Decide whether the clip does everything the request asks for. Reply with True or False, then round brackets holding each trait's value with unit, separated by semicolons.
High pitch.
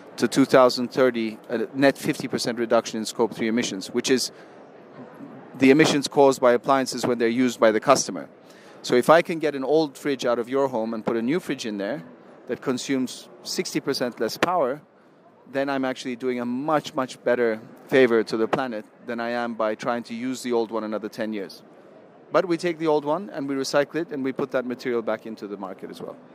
False (125 Hz)